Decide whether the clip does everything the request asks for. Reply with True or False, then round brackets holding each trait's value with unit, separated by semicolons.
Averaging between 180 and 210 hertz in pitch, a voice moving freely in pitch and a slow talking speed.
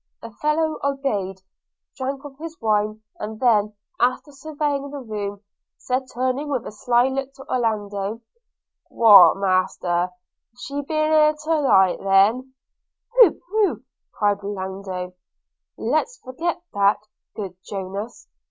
False (240 Hz; 5.9 semitones; 125 wpm)